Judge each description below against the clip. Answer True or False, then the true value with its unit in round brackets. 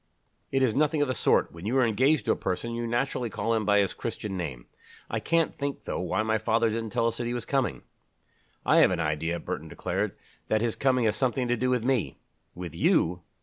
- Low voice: True (115 Hz)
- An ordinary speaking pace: False (230 wpm)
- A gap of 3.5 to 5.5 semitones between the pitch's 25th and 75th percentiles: True (4.5 semitones)